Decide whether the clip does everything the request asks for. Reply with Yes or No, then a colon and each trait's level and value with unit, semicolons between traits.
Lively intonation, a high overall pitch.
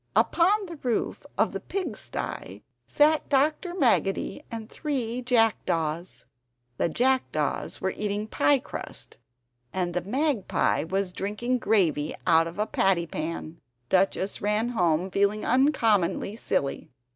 Yes: wide, 6.4 semitones; high, 210 Hz